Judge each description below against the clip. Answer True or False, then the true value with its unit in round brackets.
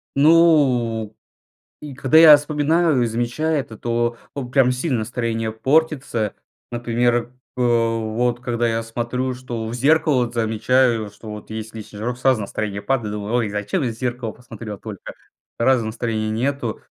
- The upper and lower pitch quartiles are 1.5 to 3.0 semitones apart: True (2.7 semitones)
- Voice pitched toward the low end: True (120 Hz)